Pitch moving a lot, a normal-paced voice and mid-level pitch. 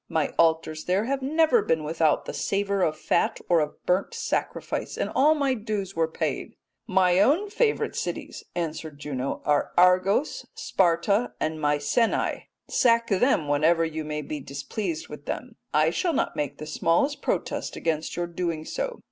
Yes: wide, 6.9 semitones; average, 165 wpm; medium, 175 Hz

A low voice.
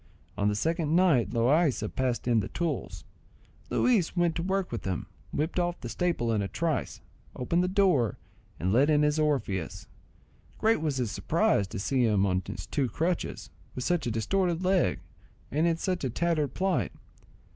No: medium, 150 Hz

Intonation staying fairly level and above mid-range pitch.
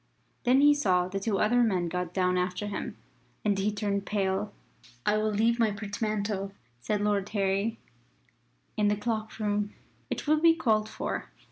Yes: narrow, 1.9 semitones; high, 210 Hz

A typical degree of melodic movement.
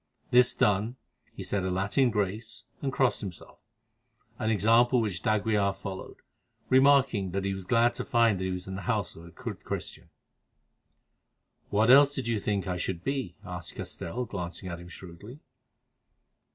Yes: average, 4.4 semitones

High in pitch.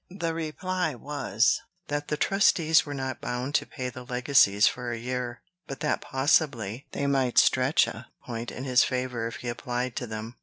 No: low, 130 Hz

